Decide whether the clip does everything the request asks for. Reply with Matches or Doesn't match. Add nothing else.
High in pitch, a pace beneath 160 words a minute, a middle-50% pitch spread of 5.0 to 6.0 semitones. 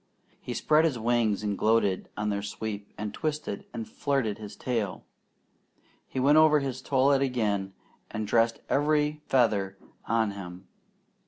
Doesn't match